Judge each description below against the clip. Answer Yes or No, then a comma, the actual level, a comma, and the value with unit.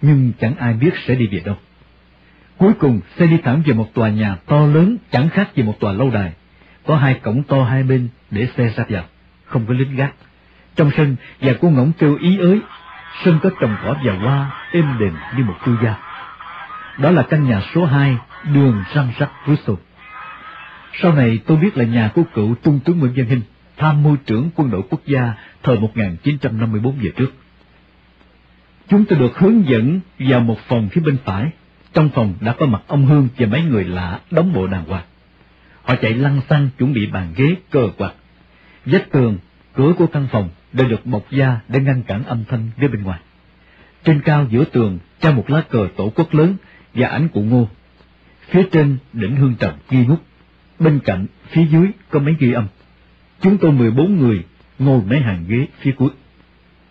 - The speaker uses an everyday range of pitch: No, wide, 6.0 semitones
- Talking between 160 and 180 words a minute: No, average, 200 wpm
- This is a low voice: Yes, low, 130 Hz